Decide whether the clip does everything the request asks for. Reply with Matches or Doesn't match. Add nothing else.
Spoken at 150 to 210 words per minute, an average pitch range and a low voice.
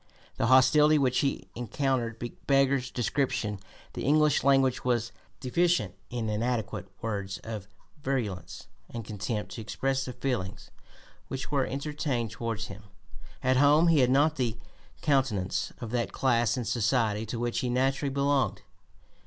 Doesn't match